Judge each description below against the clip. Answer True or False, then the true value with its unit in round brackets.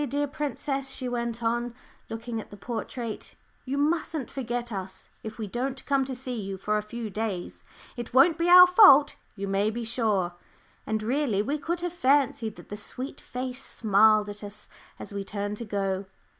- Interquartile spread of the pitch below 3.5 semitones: False (4.5 semitones)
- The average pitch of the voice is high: True (235 Hz)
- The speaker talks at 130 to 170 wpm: False (185 wpm)